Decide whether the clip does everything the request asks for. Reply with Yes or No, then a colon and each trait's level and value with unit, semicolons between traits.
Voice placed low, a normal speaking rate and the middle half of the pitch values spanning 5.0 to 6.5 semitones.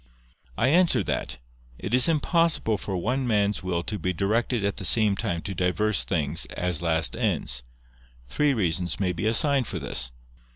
Yes: low, 100 Hz; average, 170 wpm; average, 5.3 semitones